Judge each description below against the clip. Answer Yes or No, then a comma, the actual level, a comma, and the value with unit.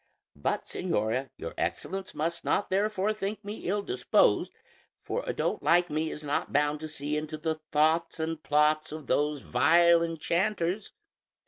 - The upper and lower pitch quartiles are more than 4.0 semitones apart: No, average, 3.5 semitones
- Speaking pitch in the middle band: Yes, medium, 160 Hz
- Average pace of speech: Yes, average, 155 wpm